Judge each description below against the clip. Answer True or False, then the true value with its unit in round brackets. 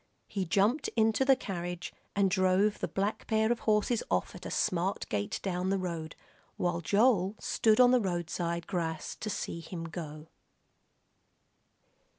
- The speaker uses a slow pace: False (155 wpm)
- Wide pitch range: False (3.9 semitones)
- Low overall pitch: False (190 Hz)